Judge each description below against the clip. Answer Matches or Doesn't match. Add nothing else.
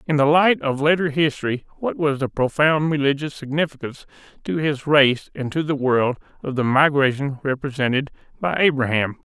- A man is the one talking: Matches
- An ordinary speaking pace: Matches